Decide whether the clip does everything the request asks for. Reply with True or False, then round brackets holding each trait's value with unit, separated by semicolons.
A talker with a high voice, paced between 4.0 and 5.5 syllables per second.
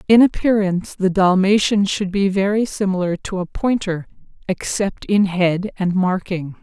True (195 Hz; 4.5 syllables/s)